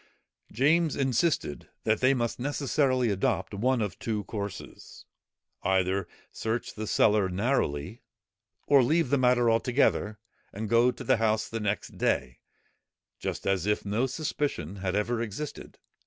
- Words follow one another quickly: No, average, 140 wpm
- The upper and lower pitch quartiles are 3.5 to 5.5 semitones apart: Yes, average, 4.3 semitones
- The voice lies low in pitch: Yes, low, 115 Hz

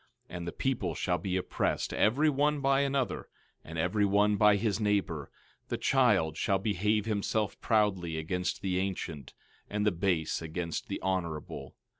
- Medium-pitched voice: No, low, 100 Hz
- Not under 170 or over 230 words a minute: No, average, 160 wpm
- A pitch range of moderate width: Yes, average, 3.7 semitones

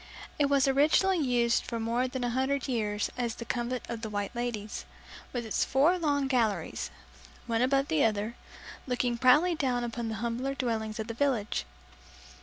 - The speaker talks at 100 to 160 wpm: No, average, 175 wpm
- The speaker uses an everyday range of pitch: Yes, average, 3.1 semitones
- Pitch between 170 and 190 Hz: No, high, 240 Hz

